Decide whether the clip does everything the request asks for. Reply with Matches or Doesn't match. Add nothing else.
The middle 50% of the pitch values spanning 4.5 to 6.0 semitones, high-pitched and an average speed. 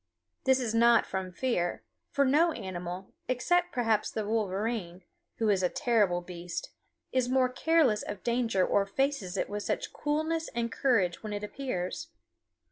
Matches